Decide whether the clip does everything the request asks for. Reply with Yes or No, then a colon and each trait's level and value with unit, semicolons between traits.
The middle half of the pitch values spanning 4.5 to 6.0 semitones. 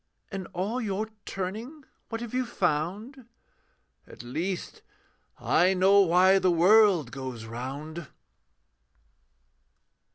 Yes: average, 5.1 semitones